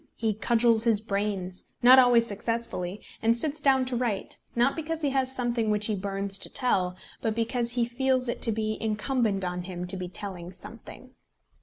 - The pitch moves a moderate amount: Yes, average, 3.8 semitones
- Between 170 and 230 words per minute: Yes, average, 185 wpm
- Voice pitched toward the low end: No, high, 225 Hz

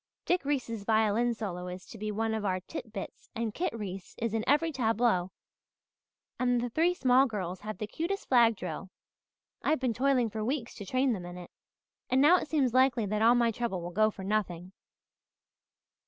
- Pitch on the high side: Yes, high, 225 Hz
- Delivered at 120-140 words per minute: No, average, 190 wpm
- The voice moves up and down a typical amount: Yes, average, 4.0 semitones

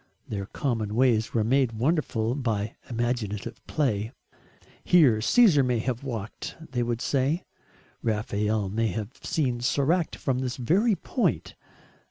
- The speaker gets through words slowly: Yes, slow, 130 wpm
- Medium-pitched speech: No, low, 120 Hz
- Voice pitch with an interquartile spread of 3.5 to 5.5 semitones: Yes, average, 3.9 semitones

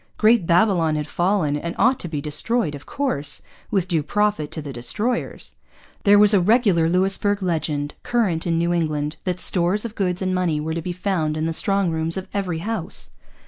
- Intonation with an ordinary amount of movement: Yes, average, 4.2 semitones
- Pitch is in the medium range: Yes, medium, 175 Hz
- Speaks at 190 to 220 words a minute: Yes, average, 195 wpm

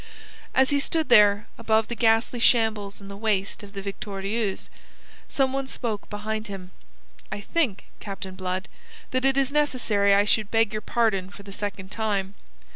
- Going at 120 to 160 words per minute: No, average, 170 wpm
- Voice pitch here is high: Yes, high, 210 Hz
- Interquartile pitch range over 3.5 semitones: No, average, 3.0 semitones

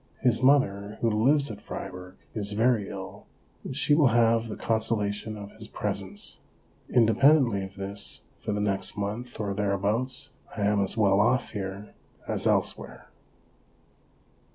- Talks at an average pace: Yes, average, 150 wpm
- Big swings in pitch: No, average, 2.8 semitones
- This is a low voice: Yes, low, 105 Hz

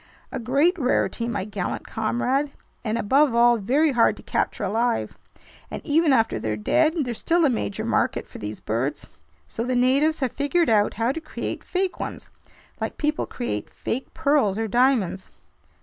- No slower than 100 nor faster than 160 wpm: No, average, 170 wpm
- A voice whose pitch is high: Yes, high, 245 Hz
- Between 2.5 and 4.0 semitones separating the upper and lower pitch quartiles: No, average, 5.2 semitones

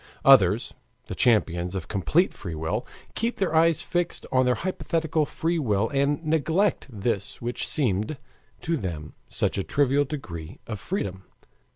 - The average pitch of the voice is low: Yes, low, 125 Hz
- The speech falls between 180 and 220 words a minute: No, average, 150 wpm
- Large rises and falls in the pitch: Yes, wide, 8.7 semitones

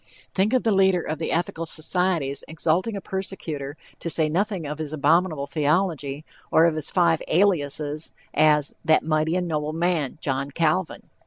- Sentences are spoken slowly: No, average, 165 wpm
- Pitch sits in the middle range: Yes, medium, 160 Hz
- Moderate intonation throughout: Yes, average, 3.1 semitones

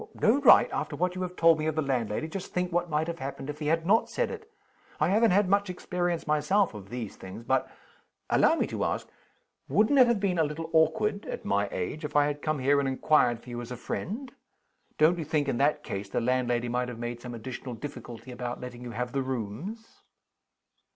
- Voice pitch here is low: No, medium, 150 Hz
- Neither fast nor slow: No, fast, 225 wpm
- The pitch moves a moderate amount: No, wide, 6.5 semitones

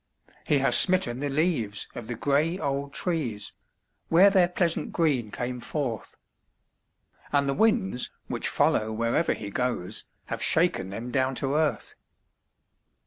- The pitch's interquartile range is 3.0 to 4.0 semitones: No, wide, 5.6 semitones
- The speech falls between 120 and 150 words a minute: Yes, average, 140 wpm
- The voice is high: No, medium, 140 Hz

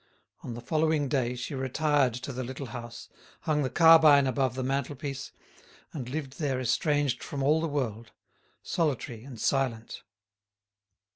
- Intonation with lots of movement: No, average, 2.8 semitones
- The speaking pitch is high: No, low, 135 Hz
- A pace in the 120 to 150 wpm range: Yes, average, 145 wpm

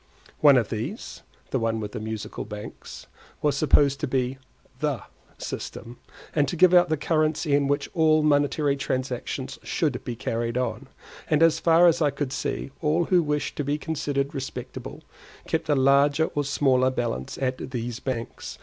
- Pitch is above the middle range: No, medium, 140 Hz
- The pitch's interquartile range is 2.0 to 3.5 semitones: Yes, average, 3.2 semitones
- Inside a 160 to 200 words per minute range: Yes, average, 170 wpm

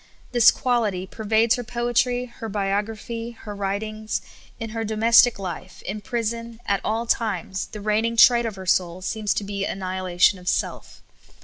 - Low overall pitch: No, high, 215 Hz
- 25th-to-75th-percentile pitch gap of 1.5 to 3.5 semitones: Yes, average, 2.9 semitones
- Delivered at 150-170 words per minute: Yes, average, 165 wpm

